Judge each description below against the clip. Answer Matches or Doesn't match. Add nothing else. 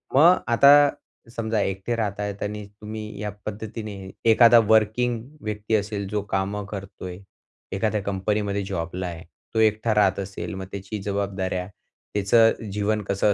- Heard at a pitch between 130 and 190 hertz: Doesn't match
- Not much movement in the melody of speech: Matches